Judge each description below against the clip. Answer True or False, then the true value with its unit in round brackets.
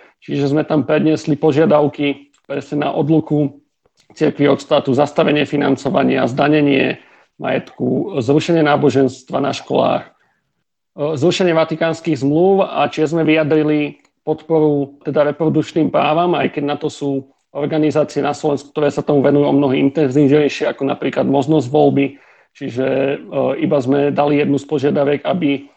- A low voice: False (145 Hz)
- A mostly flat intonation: True (1.6 semitones)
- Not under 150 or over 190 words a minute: False (135 wpm)